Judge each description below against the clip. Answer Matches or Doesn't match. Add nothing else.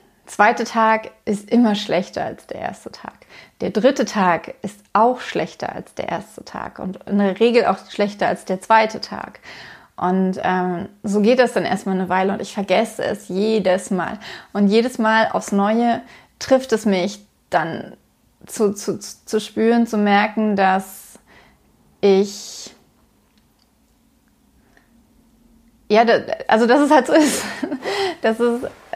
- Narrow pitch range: Doesn't match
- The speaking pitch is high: Matches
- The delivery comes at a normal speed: Matches